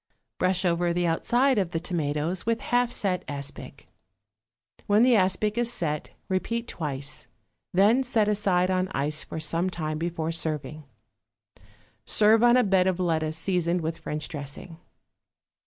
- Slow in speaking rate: No, average, 145 wpm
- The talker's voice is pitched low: No, medium, 180 Hz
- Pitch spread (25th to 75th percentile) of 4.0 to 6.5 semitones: Yes, average, 4.7 semitones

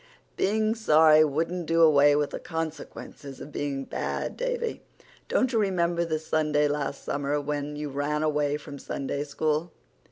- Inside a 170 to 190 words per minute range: No, average, 155 wpm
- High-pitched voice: No, medium, 150 Hz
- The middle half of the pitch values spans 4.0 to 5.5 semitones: No, narrow, 2.5 semitones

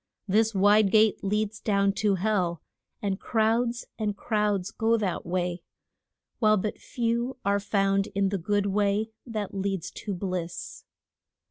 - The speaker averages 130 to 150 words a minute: Yes, average, 140 wpm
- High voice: Yes, high, 205 Hz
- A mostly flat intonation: Yes, narrow, 1.9 semitones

